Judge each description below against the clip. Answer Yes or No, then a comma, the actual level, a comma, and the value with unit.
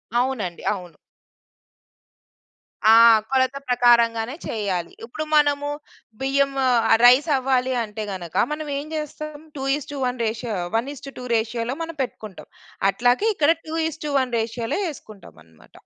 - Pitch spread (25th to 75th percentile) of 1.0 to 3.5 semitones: No, average, 4.1 semitones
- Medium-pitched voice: No, very high, 250 Hz